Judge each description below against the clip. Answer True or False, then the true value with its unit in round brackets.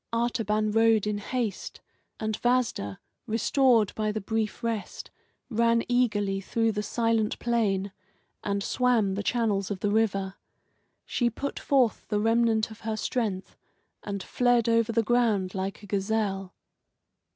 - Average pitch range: False (2.3 semitones)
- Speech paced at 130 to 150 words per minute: True (140 wpm)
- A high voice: True (220 Hz)